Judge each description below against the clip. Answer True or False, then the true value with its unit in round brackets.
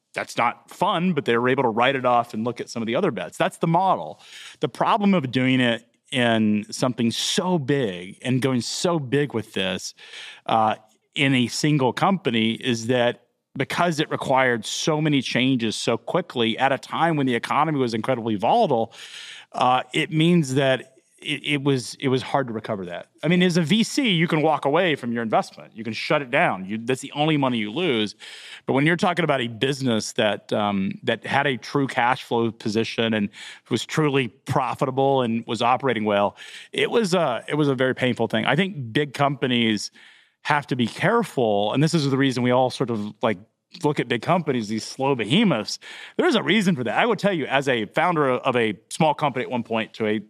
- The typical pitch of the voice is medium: False (130 Hz)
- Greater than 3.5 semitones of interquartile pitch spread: True (4.3 semitones)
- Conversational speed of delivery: False (210 wpm)